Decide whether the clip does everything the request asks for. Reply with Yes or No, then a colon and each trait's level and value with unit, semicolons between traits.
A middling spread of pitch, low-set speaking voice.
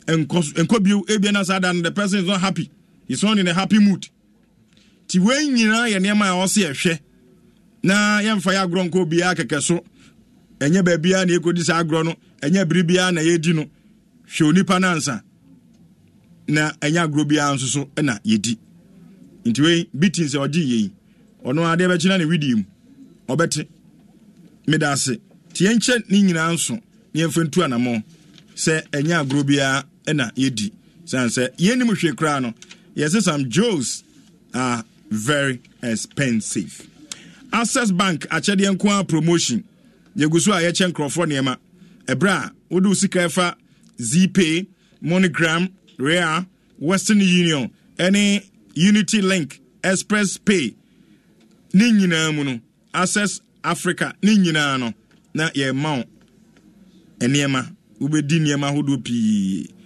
No: average, 4.4 semitones; medium, 175 Hz